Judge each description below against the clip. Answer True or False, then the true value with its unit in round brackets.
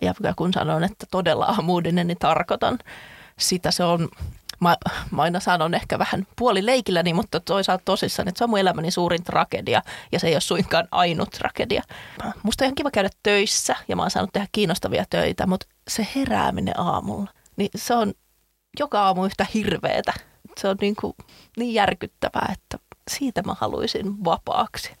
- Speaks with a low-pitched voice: False (195 Hz)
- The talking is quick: True (170 wpm)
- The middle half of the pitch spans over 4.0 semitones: False (3.2 semitones)